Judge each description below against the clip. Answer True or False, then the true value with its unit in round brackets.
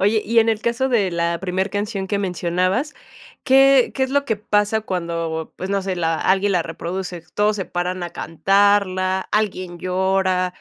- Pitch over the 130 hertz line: True (190 Hz)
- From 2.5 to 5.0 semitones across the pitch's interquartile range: True (2.8 semitones)